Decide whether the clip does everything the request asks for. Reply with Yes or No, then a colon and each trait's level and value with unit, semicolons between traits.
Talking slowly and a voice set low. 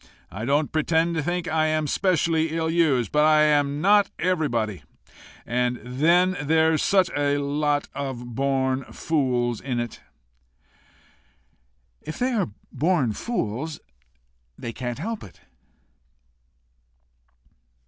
No: slow, 115 wpm; medium, 150 Hz